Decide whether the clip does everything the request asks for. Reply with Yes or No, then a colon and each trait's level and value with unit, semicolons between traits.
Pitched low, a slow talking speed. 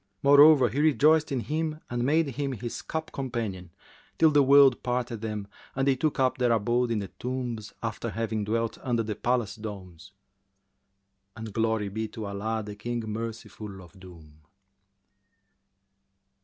No: low, 115 Hz; average, 155 wpm